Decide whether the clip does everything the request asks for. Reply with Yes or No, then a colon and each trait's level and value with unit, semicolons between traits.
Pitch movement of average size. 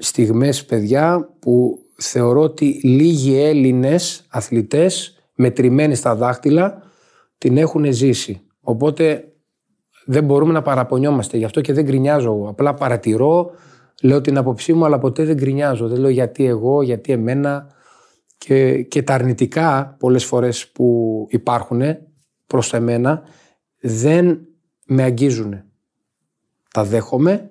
Yes: average, 3.7 semitones